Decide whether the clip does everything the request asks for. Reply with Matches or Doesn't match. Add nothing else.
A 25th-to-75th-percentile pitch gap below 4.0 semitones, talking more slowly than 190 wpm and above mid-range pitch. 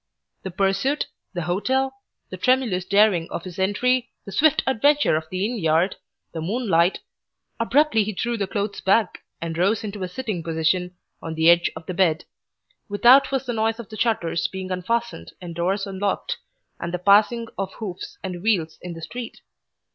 Doesn't match